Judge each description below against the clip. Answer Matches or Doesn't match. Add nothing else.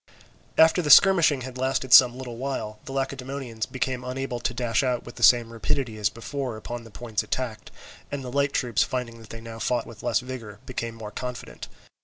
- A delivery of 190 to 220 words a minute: Matches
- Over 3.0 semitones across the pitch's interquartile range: Doesn't match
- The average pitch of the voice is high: Doesn't match